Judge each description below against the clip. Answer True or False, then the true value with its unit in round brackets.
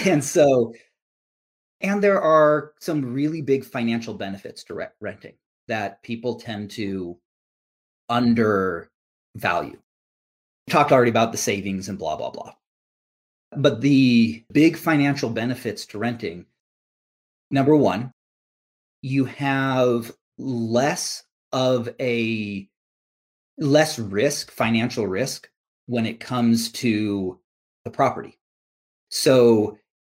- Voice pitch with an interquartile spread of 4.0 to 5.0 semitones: True (4.6 semitones)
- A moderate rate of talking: False (105 wpm)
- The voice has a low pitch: True (120 Hz)